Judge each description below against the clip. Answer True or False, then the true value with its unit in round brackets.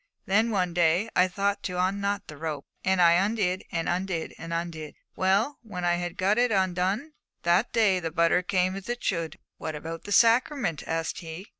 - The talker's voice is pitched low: False (185 Hz)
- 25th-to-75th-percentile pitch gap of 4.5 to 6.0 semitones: False (3.2 semitones)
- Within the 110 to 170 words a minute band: False (195 wpm)